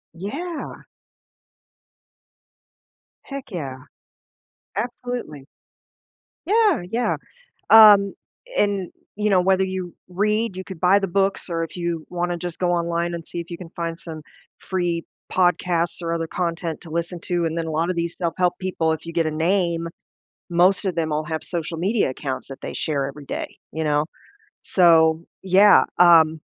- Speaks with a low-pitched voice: No, medium, 175 Hz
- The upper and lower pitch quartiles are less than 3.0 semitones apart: Yes, narrow, 2.5 semitones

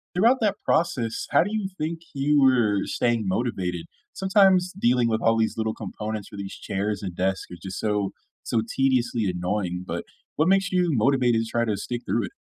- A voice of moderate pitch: No, low, 115 Hz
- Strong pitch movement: Yes, wide, 6.5 semitones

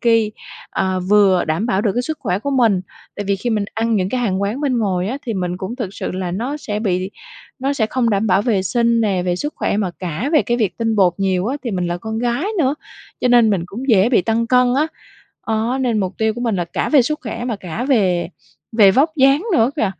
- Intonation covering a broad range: No, average, 4.4 semitones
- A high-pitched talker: Yes, high, 220 Hz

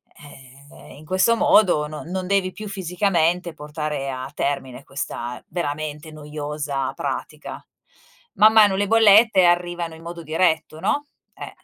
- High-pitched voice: No, medium, 160 Hz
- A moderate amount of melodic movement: Yes, average, 4.2 semitones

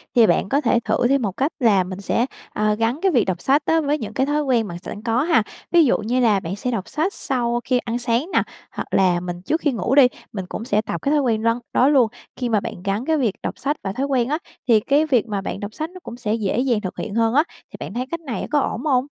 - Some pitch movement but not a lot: Yes, average, 4.7 semitones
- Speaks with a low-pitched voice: No, high, 240 Hz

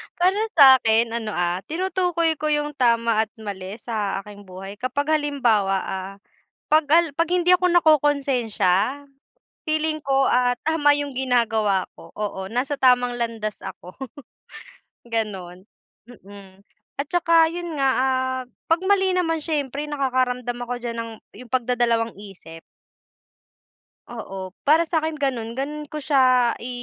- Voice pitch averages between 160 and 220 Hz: No, very high, 255 Hz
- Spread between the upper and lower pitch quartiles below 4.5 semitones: No, wide, 5.6 semitones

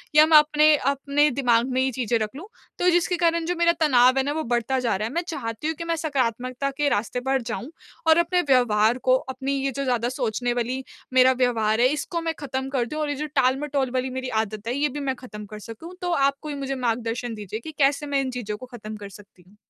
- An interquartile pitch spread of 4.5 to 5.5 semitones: No, average, 3.8 semitones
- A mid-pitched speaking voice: No, very high, 260 Hz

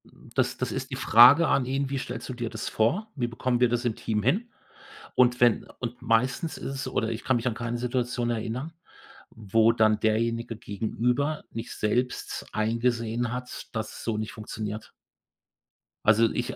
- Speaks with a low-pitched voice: Yes, low, 120 Hz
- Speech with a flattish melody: Yes, narrow, 2.1 semitones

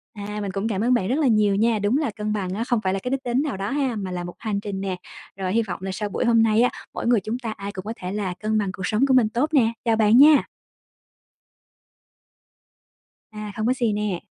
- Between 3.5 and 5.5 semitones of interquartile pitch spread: No, average, 3.1 semitones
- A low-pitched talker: No, high, 215 Hz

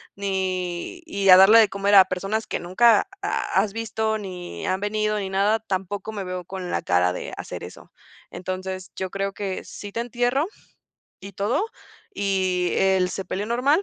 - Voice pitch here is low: No, high, 195 Hz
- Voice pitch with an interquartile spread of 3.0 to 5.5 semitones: No, narrow, 2.4 semitones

